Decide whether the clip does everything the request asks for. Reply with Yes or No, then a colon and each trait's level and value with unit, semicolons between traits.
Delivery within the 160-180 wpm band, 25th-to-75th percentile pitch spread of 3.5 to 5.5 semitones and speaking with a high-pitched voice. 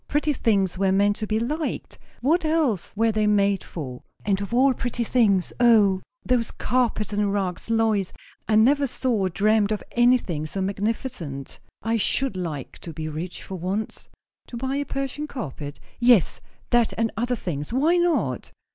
Yes: average, 170 wpm; average, 4.7 semitones; high, 215 Hz